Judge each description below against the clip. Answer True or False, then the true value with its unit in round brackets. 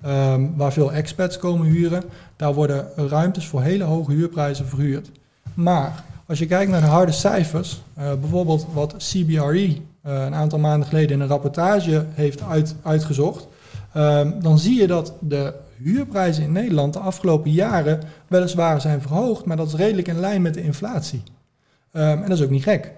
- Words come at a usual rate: True (180 wpm)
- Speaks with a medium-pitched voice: True (155 Hz)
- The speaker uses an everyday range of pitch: True (3.4 semitones)